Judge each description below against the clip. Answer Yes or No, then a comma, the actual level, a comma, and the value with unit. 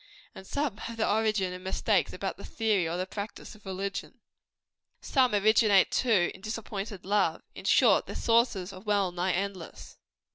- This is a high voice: Yes, high, 200 Hz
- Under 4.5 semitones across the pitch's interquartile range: Yes, average, 2.8 semitones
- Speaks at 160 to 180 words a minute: Yes, average, 170 wpm